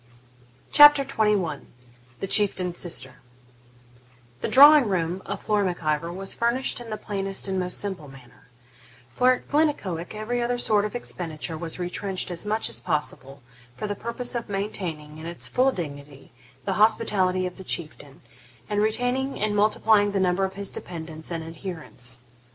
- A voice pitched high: Yes, high, 195 Hz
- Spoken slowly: No, average, 160 wpm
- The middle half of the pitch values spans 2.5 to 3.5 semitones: No, average, 4.6 semitones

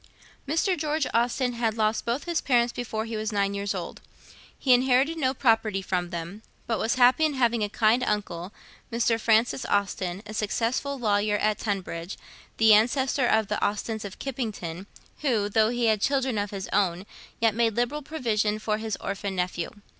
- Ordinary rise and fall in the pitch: Yes, average, 3.4 semitones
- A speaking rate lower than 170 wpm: No, average, 175 wpm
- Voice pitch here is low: No, high, 220 Hz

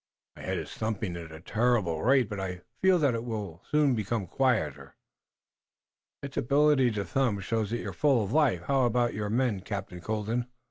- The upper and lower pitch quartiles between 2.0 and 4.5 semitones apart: No, average, 4.9 semitones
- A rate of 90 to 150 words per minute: No, average, 185 wpm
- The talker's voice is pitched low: Yes, low, 110 Hz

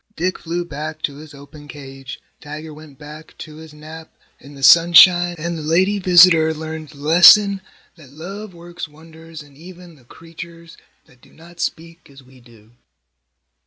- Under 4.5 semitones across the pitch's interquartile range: Yes, average, 2.7 semitones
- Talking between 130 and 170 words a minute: Yes, average, 165 wpm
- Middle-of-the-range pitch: Yes, medium, 160 Hz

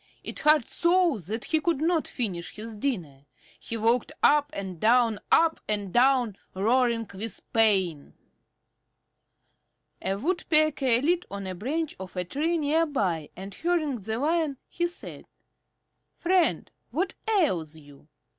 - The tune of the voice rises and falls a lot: Yes, wide, 8.1 semitones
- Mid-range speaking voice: No, high, 240 Hz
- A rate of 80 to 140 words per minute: Yes, slow, 135 wpm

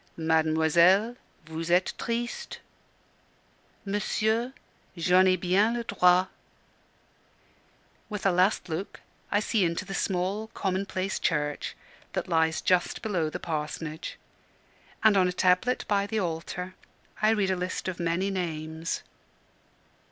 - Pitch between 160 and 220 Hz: Yes, medium, 185 Hz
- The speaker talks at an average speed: No, slow, 120 wpm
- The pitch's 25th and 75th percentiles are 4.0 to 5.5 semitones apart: No, average, 3.4 semitones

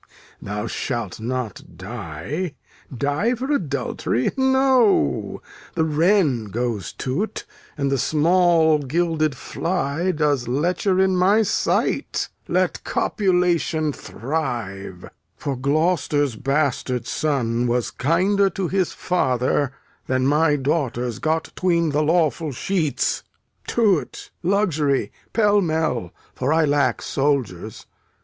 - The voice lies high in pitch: No, medium, 150 Hz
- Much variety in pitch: Yes, wide, 5.8 semitones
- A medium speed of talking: No, slow, 105 wpm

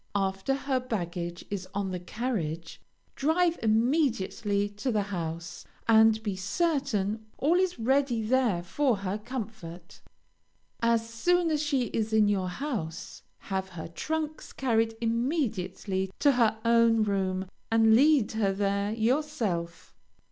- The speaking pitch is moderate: No, high, 220 Hz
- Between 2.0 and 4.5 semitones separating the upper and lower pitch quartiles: No, average, 5.3 semitones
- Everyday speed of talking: No, slow, 130 wpm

